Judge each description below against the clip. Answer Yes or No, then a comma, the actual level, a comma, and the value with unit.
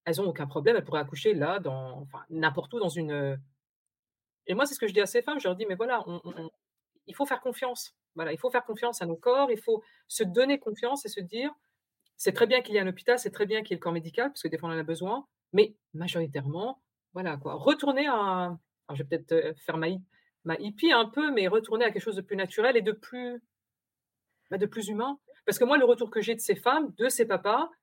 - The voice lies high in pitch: Yes, high, 215 Hz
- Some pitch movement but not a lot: No, wide, 6.8 semitones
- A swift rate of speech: Yes, fast, 265 wpm